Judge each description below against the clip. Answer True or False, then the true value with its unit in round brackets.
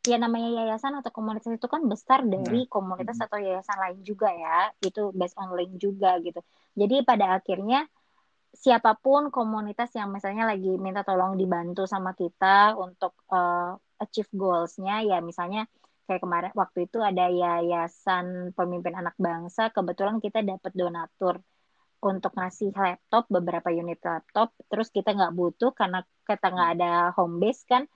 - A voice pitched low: False (195 Hz)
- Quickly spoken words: True (150 wpm)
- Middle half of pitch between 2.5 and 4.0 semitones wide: True (3.6 semitones)